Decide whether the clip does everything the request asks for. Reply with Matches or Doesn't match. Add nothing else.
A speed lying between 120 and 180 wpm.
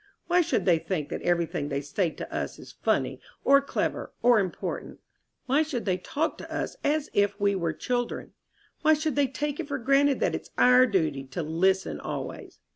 Doesn't match